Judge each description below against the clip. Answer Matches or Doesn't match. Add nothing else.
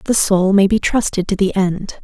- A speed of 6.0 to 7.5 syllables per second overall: Doesn't match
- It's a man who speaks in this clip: Doesn't match